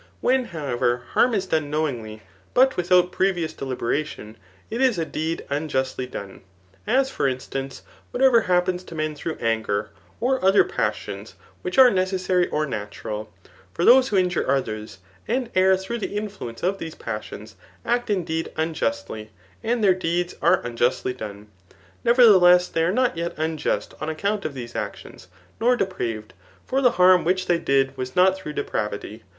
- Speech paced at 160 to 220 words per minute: Yes, average, 165 wpm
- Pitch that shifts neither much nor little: No, wide, 7.2 semitones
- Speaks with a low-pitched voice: No, medium, 170 Hz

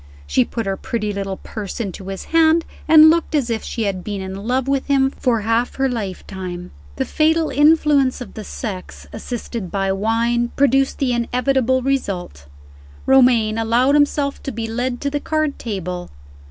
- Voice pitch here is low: No, high, 235 Hz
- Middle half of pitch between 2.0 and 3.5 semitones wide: No, average, 5.3 semitones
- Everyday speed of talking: Yes, average, 170 wpm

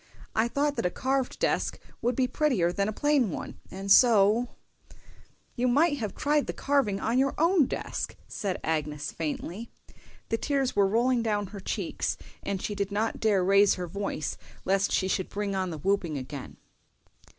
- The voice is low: No, high, 205 Hz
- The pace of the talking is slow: No, average, 175 wpm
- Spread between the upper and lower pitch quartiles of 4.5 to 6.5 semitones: Yes, average, 4.9 semitones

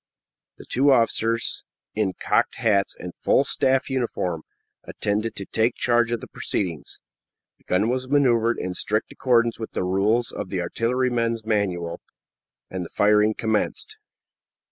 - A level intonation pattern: No, average, 3.3 semitones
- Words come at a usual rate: Yes, average, 145 wpm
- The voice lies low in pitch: Yes, low, 110 Hz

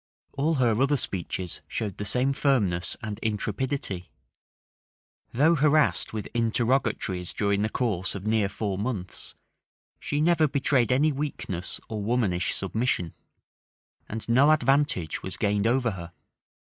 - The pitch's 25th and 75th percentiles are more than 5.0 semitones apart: Yes, wide, 5.6 semitones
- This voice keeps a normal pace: No, slow, 130 wpm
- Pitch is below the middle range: Yes, low, 115 Hz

